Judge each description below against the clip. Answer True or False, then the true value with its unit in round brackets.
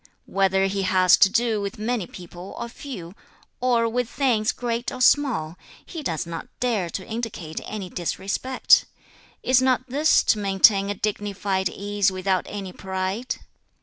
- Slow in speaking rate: False (150 wpm)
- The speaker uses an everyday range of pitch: True (4.3 semitones)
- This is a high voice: True (205 Hz)